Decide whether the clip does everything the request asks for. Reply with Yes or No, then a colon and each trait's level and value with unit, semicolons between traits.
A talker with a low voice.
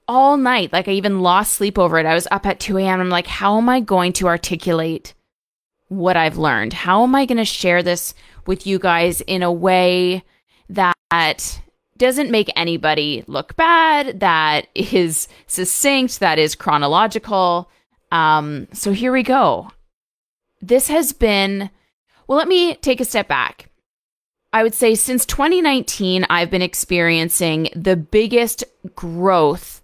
No: high, 190 Hz